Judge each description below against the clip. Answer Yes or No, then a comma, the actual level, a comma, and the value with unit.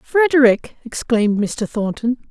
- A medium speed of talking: No, slow, 105 wpm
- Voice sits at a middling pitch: No, high, 245 Hz